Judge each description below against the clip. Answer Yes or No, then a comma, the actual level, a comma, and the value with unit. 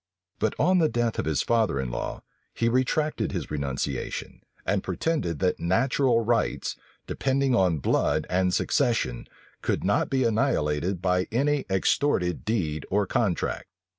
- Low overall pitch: Yes, low, 110 Hz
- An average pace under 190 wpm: Yes, average, 140 wpm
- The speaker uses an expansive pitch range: Yes, wide, 6.9 semitones